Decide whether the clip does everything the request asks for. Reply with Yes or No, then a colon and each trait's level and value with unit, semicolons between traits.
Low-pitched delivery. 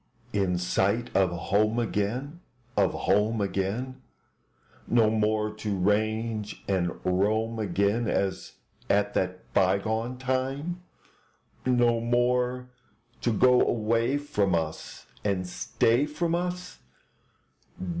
Yes: low, 110 Hz